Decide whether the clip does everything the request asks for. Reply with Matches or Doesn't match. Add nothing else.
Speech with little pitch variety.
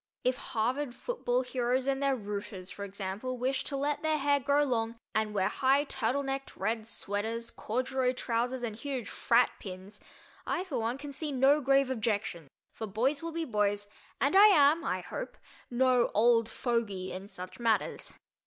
Doesn't match